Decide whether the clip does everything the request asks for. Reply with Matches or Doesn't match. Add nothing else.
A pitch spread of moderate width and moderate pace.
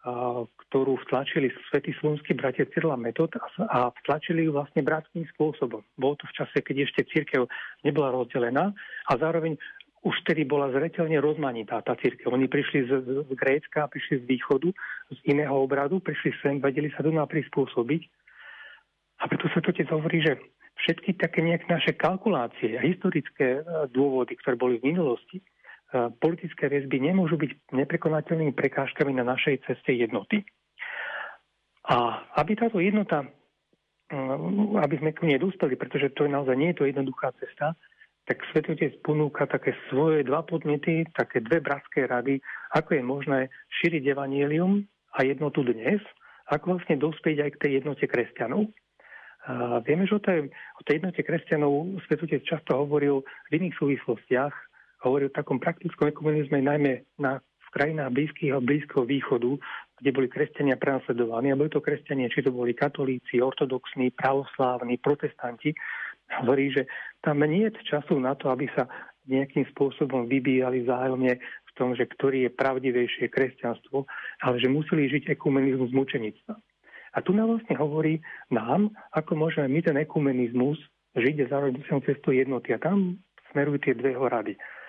Matches